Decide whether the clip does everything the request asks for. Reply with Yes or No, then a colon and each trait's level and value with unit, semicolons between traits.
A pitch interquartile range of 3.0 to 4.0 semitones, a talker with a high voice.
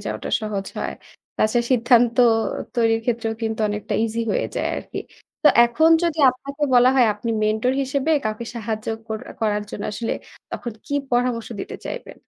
No: narrow, 2.5 semitones; high, 230 Hz